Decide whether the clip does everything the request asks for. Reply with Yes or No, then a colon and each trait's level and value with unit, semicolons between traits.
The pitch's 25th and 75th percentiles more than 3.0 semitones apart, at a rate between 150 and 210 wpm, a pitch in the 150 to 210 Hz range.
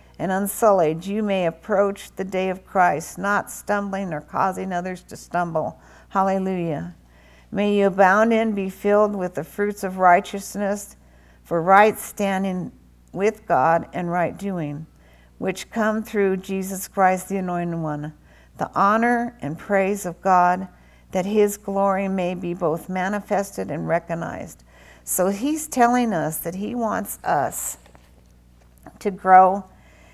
No: average, 3.7 semitones; slow, 135 wpm; medium, 185 Hz